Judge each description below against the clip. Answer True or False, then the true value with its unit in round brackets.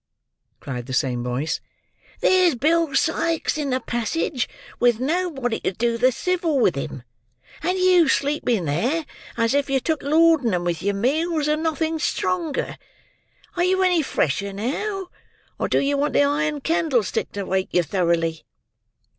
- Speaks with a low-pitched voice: False (275 Hz)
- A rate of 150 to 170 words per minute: True (155 wpm)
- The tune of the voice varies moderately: False (8.4 semitones)